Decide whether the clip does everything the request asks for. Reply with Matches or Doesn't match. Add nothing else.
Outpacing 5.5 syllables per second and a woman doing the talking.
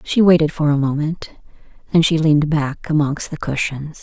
Doesn't match